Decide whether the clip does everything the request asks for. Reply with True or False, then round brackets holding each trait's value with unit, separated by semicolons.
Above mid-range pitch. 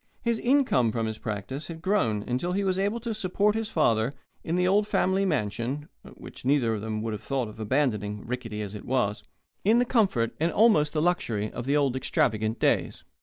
False (135 Hz)